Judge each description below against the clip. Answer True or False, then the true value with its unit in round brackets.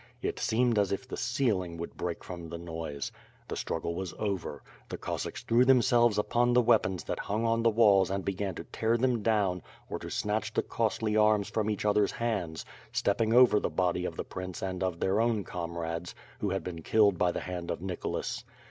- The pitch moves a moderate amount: True (4.1 semitones)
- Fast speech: True (210 wpm)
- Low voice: True (100 Hz)